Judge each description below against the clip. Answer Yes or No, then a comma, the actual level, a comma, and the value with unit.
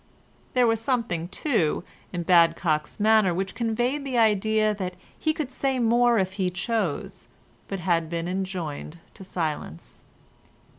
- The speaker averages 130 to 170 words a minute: Yes, average, 140 wpm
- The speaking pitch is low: No, high, 195 Hz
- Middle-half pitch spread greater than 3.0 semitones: Yes, average, 5.1 semitones